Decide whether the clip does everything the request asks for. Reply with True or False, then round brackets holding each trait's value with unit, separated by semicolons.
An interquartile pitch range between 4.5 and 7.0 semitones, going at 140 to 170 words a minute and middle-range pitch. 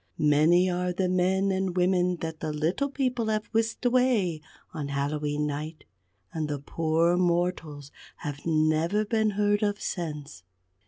True (4.8 semitones; 145 wpm; 175 Hz)